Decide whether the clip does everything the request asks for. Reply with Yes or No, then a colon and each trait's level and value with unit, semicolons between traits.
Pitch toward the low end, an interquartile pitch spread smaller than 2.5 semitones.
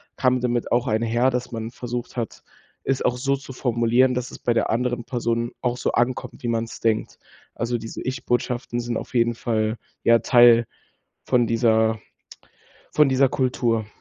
Yes: low, 120 Hz; narrow, 1.3 semitones